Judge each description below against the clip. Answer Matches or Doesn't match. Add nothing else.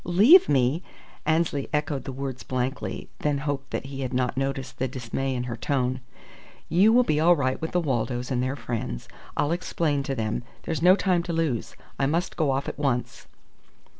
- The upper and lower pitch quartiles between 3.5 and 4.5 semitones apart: Matches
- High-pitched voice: Doesn't match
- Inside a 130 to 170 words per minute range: Doesn't match